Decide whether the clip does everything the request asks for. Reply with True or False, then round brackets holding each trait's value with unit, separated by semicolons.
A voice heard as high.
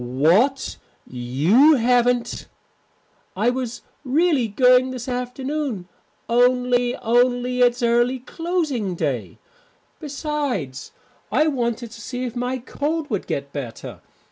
True (245 Hz)